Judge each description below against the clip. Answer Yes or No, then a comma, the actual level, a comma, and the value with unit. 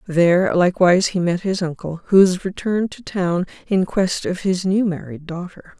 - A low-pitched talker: No, medium, 180 Hz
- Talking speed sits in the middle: Yes, average, 185 wpm